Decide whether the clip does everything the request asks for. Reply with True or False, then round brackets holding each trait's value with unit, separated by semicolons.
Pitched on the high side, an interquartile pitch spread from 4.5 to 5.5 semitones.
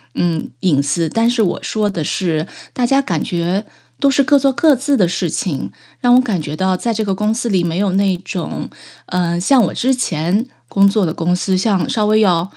True (195 Hz; 5.1 semitones)